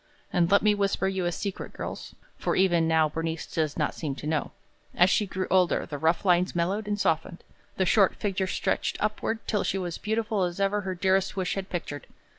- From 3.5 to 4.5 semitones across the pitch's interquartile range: No, average, 2.8 semitones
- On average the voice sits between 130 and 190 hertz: Yes, medium, 185 Hz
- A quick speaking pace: Yes, fast, 210 wpm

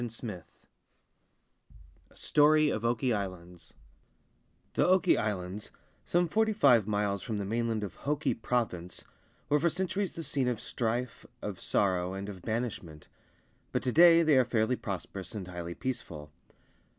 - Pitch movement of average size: No, wide, 6.9 semitones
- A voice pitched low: Yes, low, 115 Hz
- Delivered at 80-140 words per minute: No, average, 150 wpm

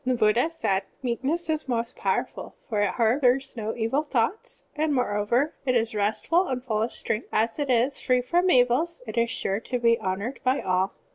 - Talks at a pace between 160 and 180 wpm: No, average, 195 wpm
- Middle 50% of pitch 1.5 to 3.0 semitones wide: No, average, 3.8 semitones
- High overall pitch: Yes, high, 245 Hz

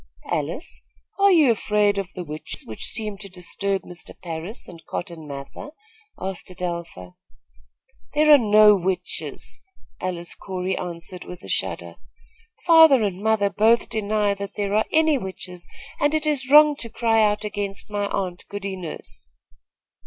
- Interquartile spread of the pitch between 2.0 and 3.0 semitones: No, average, 3.7 semitones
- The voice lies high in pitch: Yes, high, 200 Hz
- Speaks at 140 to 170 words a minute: Yes, average, 150 wpm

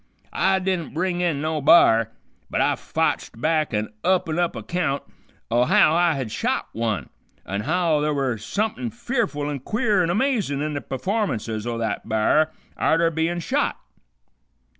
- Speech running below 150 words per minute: No, average, 160 wpm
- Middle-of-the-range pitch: Yes, medium, 155 Hz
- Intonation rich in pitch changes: Yes, wide, 6.6 semitones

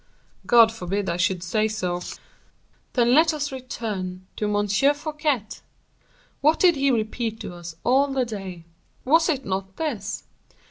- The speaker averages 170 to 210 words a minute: No, average, 145 wpm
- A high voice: Yes, high, 225 Hz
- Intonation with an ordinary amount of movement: No, wide, 6.3 semitones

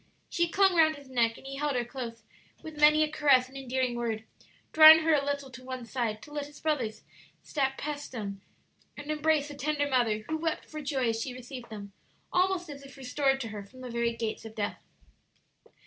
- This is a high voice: Yes, very high, 270 Hz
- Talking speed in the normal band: No, fast, 210 wpm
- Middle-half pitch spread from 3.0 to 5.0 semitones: Yes, average, 4.1 semitones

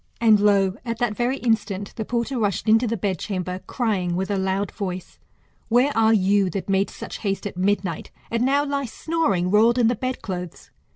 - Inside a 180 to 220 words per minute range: Yes, average, 195 wpm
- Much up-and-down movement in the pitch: No, average, 3.7 semitones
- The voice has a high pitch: Yes, high, 210 Hz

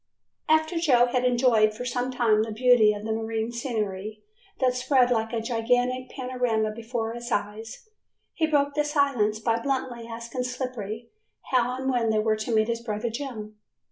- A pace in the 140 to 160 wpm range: No, average, 175 wpm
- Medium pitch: No, high, 235 Hz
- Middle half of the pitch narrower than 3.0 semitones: Yes, narrow, 2.4 semitones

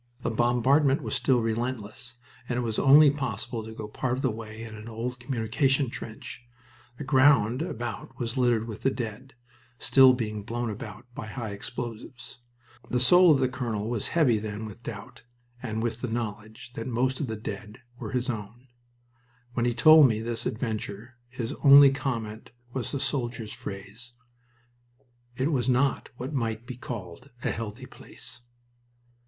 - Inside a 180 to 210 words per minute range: No, average, 170 wpm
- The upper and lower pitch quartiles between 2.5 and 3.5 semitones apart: Yes, average, 2.9 semitones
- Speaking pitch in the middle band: No, low, 120 Hz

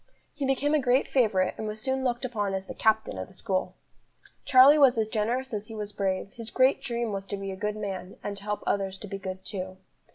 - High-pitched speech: Yes, high, 215 Hz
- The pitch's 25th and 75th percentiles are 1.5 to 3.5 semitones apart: No, average, 4.1 semitones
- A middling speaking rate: No, fast, 245 wpm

